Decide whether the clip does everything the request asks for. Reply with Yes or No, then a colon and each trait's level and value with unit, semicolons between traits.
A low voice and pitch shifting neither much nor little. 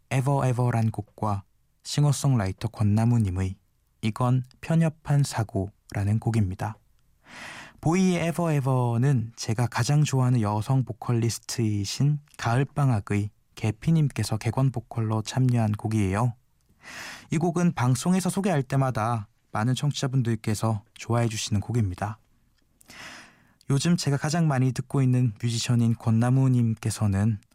Yes: low, 120 Hz; average, 3.6 semitones